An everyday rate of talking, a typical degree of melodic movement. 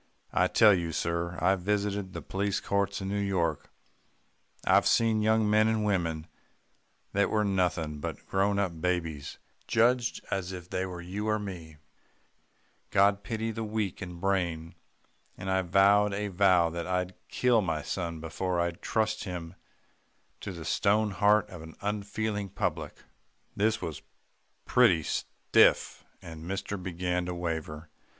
Yes: average, 150 wpm; average, 3.1 semitones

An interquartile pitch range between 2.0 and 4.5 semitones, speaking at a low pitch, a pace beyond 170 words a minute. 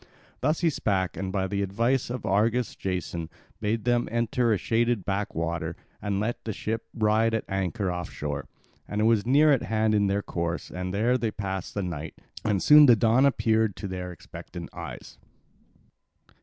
Yes: average, 3.6 semitones; low, 105 Hz; average, 180 wpm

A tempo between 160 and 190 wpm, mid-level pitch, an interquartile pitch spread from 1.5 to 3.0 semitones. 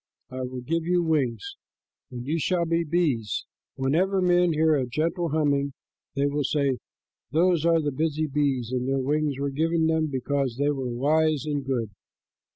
No: average, 170 wpm; medium, 150 Hz; average, 3.4 semitones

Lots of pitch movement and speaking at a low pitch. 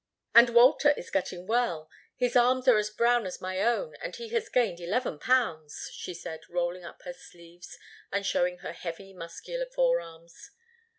No: wide, 6.4 semitones; high, 200 Hz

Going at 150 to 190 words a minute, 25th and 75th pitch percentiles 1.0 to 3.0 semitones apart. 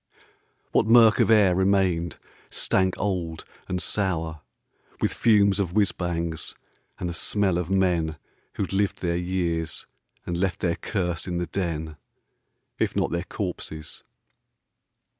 No: slow, 135 wpm; narrow, 2.5 semitones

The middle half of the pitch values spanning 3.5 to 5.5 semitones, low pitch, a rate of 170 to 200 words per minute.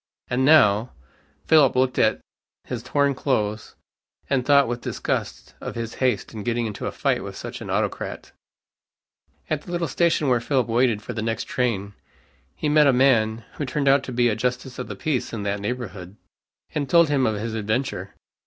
Yes: average, 3.9 semitones; low, 125 Hz; average, 185 wpm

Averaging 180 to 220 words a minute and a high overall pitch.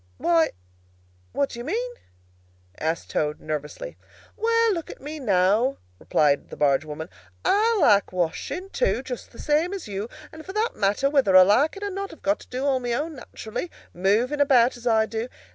Yes: average, 195 wpm; very high, 255 Hz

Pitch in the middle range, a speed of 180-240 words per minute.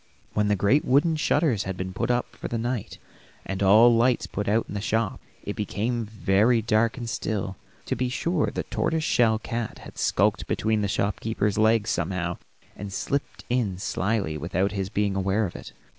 No: low, 105 Hz; average, 190 wpm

